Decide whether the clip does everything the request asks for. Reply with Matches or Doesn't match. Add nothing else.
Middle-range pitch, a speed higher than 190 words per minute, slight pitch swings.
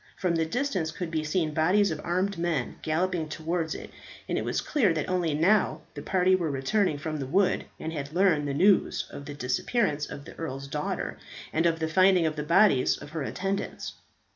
Doesn't match